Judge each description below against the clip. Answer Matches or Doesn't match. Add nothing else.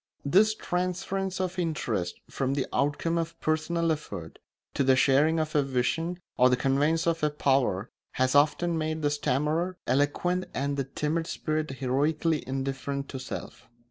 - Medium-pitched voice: Matches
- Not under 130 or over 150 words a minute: Doesn't match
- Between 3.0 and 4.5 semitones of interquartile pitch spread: Matches